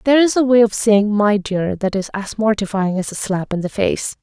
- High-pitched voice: Yes, high, 210 Hz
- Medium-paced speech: No, fast, 255 wpm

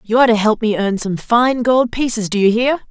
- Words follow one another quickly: Yes, fast, 270 wpm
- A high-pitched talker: Yes, high, 225 Hz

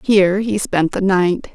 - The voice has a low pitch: No, high, 190 Hz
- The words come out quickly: No, average, 195 wpm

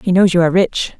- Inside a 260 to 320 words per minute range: Yes, fast, 305 wpm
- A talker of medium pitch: Yes, medium, 180 Hz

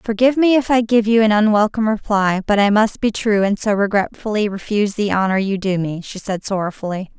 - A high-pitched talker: Yes, high, 210 Hz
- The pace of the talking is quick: Yes, fast, 215 wpm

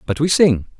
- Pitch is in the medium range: Yes, medium, 145 Hz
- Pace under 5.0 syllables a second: No, 5.4 syllables/s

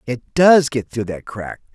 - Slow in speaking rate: No, fast, 205 wpm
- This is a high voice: No, low, 125 Hz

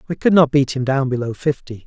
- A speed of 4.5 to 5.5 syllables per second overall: No, 5.9 syllables/s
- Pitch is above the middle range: No, low, 135 Hz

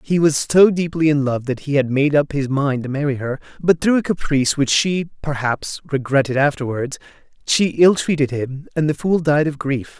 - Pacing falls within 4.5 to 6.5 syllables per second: Yes, 5.0 syllables/s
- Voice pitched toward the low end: No, medium, 145 Hz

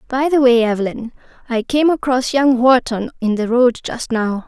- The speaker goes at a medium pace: Yes, average, 190 wpm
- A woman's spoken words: Yes, female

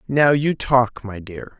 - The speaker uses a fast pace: No, average, 190 wpm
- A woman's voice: No, male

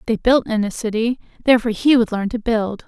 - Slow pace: No, fast, 230 wpm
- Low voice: No, high, 225 Hz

